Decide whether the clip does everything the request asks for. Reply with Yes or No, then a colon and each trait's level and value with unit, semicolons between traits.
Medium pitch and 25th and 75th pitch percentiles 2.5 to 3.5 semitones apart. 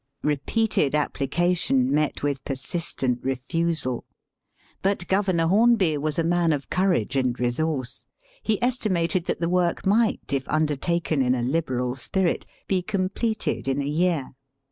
No: medium, 160 Hz; average, 5.1 semitones